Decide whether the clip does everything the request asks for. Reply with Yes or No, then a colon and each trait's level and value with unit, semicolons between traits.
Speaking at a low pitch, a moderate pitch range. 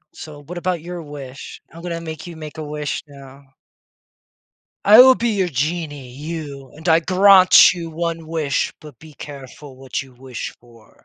No: medium, 155 Hz; average, 3.5 semitones